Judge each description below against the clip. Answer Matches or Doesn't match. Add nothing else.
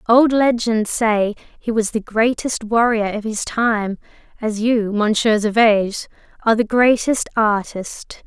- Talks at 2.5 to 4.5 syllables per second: Matches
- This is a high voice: Matches